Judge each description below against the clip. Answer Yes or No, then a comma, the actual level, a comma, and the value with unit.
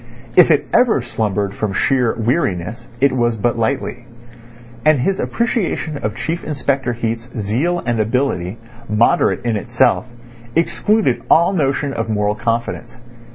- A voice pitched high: No, low, 120 Hz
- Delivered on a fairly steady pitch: No, average, 4.1 semitones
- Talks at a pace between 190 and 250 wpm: No, slow, 135 wpm